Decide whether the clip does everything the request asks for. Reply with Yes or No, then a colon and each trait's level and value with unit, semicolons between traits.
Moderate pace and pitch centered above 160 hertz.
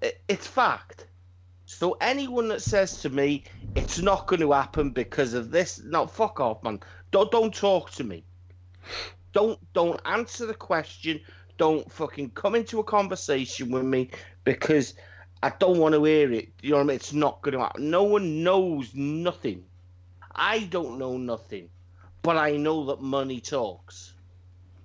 No: average, 165 wpm; medium, 140 Hz